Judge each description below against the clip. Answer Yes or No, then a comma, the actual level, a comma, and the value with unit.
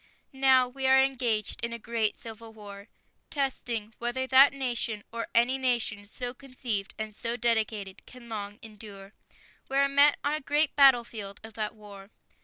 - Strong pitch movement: No, average, 3.6 semitones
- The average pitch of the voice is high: Yes, high, 235 Hz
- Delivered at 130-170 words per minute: Yes, average, 165 wpm